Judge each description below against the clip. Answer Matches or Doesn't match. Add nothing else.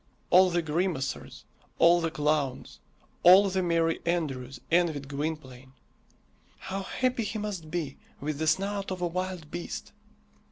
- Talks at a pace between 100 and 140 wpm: Matches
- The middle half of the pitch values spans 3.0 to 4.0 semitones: Matches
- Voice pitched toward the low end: Doesn't match